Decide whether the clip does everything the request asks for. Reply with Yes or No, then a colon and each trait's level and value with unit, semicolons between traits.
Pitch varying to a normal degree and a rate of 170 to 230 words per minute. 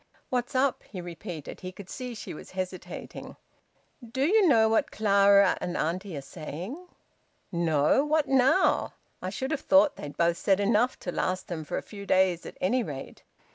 No: wide, 6.3 semitones; average, 175 wpm